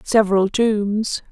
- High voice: Yes, high, 210 Hz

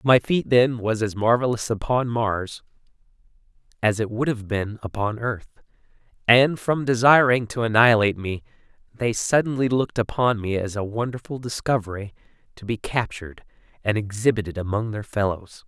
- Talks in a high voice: No, low, 115 Hz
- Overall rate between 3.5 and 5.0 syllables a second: No, 5.2 syllables/s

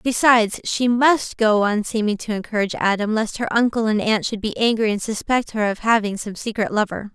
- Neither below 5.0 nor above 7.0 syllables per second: Yes, 5.4 syllables/s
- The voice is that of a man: No, female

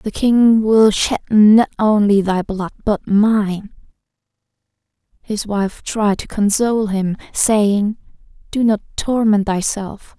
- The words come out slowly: Yes, slow, 125 wpm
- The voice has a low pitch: No, high, 210 Hz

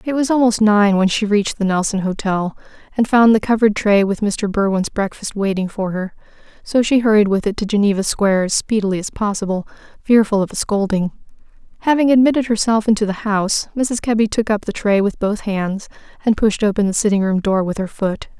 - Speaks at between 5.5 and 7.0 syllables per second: Yes, 5.7 syllables/s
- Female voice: Yes, female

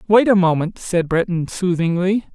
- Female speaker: No, male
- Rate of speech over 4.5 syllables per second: Yes, 4.7 syllables/s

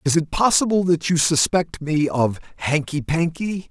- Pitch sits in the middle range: Yes, medium, 160 Hz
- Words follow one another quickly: No, average, 160 wpm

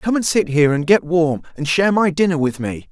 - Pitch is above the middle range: No, medium, 165 Hz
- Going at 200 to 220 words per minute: No, fast, 265 wpm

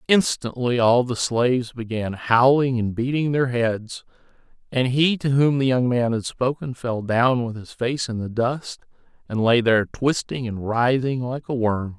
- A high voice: No, low, 125 Hz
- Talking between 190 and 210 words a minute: No, average, 180 wpm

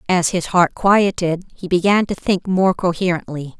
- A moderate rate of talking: Yes, average, 165 wpm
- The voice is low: No, medium, 180 Hz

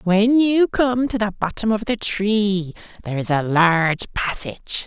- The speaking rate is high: No, average, 175 wpm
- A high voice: Yes, high, 205 Hz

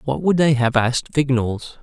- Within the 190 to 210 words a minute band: Yes, average, 200 wpm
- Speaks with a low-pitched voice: Yes, low, 130 Hz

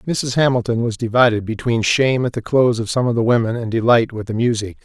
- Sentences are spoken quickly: Yes, fast, 235 wpm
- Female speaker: No, male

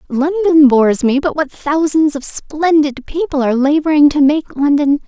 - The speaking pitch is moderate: No, very high, 295 Hz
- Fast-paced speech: No, average, 165 wpm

